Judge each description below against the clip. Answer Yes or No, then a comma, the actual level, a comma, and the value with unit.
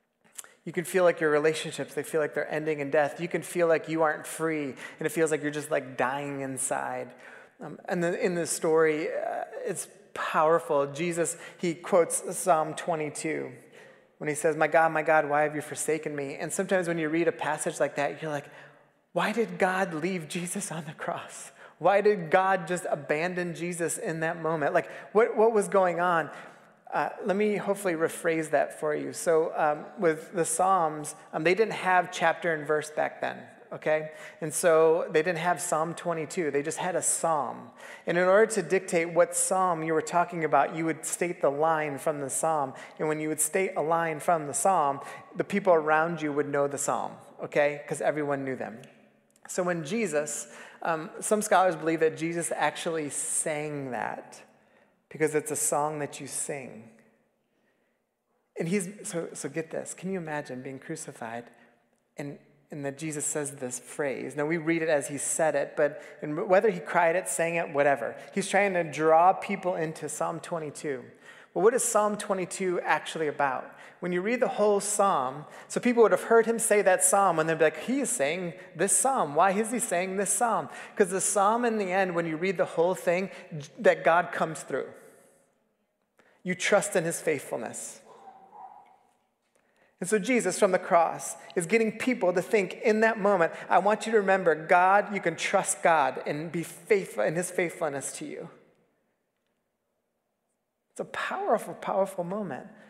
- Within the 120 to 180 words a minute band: No, average, 190 wpm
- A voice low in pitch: No, medium, 170 Hz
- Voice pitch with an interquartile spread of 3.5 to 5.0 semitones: Yes, average, 3.8 semitones